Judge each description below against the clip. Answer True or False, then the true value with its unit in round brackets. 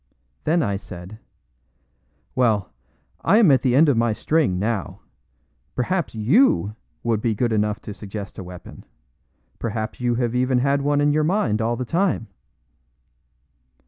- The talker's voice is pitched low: True (120 Hz)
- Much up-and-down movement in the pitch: False (5.0 semitones)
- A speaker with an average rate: True (150 wpm)